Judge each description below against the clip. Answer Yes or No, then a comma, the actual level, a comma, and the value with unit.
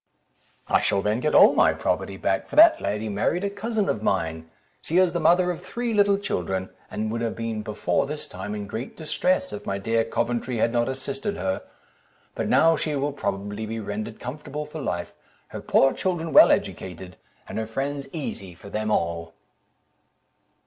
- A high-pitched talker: No, low, 115 Hz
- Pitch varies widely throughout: Yes, wide, 8.0 semitones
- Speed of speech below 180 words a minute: No, average, 185 wpm